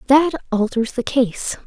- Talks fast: No, average, 145 wpm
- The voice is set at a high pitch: Yes, very high, 250 Hz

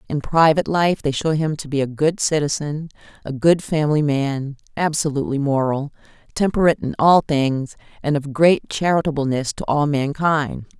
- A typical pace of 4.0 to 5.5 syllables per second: Yes, 5.1 syllables/s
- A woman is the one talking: Yes, female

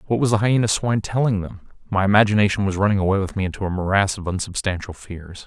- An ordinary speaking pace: No, fast, 220 wpm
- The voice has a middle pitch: No, low, 100 Hz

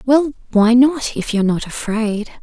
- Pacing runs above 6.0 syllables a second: No, 4.6 syllables/s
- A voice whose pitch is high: Yes, high, 235 Hz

